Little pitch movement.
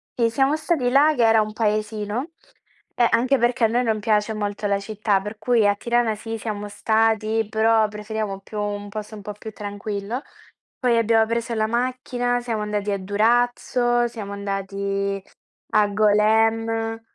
Yes: narrow, 2.2 semitones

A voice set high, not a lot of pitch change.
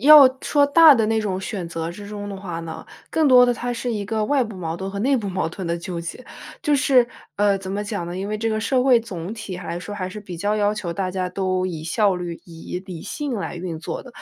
No: high, 200 Hz; average, 4.3 semitones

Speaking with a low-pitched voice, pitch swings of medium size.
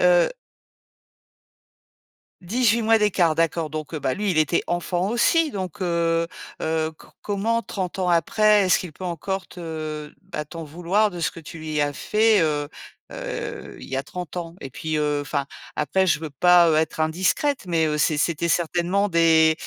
No: medium, 170 Hz; average, 3.3 semitones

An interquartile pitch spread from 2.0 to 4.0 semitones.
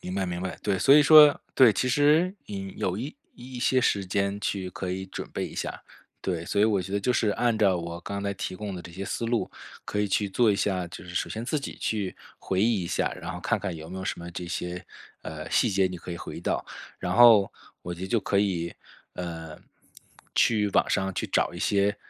Yes: average, 3.5 semitones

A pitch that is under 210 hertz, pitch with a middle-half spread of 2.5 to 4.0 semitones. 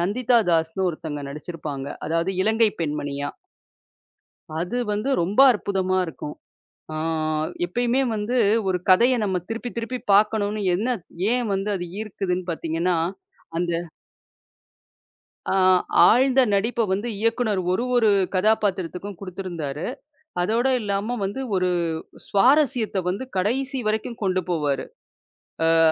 No: high, 200 Hz; average, 4.7 semitones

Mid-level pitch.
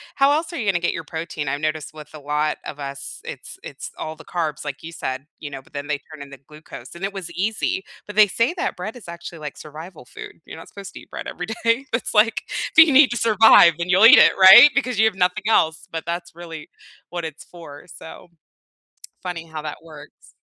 Yes: medium, 170 Hz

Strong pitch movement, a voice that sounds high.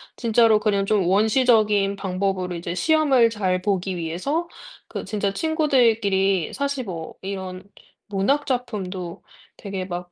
No: average, 4.2 semitones; high, 200 Hz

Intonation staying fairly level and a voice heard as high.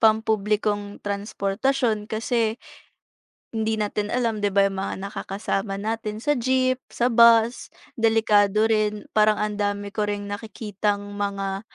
Yes: narrow, 1.7 semitones; high, 210 Hz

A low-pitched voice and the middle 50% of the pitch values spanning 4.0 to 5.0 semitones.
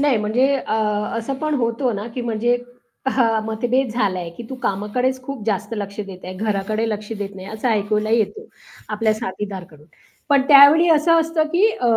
No: high, 225 Hz; average, 4.3 semitones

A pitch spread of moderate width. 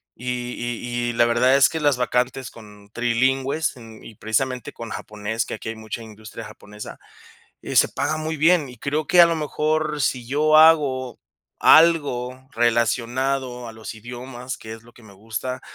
Yes: average, 3.5 semitones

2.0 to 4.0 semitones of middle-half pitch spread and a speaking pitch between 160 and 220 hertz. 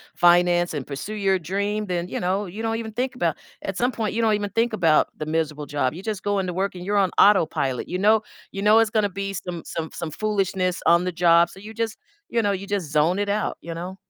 Yes: average, 3.4 semitones; high, 190 Hz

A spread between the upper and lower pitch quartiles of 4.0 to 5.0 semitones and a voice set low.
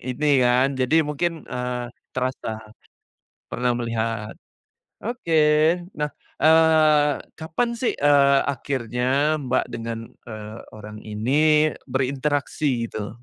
Yes: average, 4.5 semitones; low, 130 Hz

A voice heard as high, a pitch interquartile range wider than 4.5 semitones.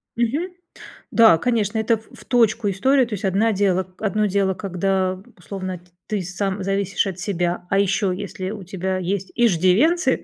No: high, 195 Hz; average, 2.9 semitones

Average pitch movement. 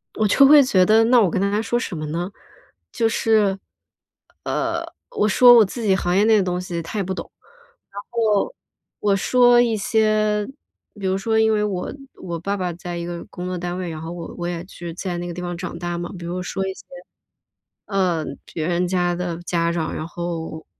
Yes: average, 3.5 semitones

